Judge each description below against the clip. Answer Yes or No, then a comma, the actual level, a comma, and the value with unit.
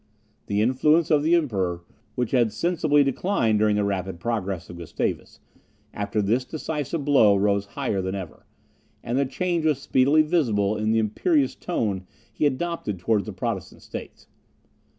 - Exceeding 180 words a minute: No, average, 155 wpm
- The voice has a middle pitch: No, low, 115 Hz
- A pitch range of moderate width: No, wide, 7.0 semitones